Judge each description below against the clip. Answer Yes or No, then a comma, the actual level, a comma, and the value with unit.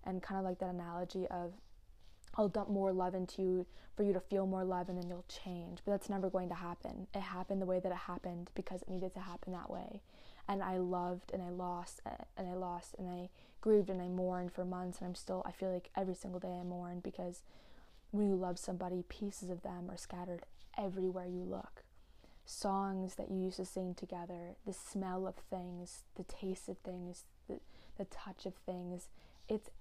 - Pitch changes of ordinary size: No, narrow, 1.2 semitones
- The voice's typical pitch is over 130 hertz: Yes, medium, 185 Hz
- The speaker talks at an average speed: No, fast, 210 wpm